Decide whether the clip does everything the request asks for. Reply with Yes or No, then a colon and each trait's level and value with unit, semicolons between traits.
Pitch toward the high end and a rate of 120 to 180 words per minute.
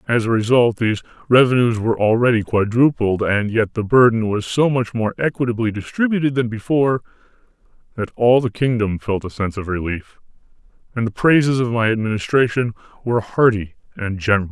No: low, 115 Hz; average, 160 wpm